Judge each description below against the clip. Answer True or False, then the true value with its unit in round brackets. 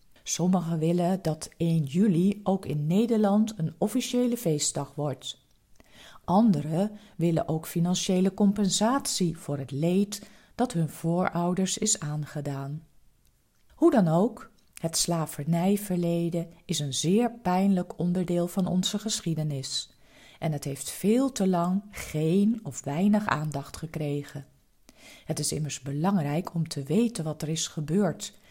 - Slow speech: True (125 wpm)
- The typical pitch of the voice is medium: True (170 Hz)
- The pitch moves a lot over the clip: False (4.6 semitones)